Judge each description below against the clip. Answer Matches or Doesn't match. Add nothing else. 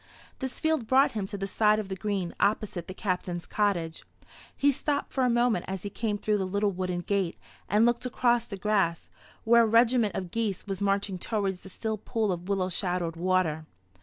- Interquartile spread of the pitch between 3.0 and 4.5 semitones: Matches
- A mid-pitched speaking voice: Doesn't match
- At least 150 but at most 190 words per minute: Doesn't match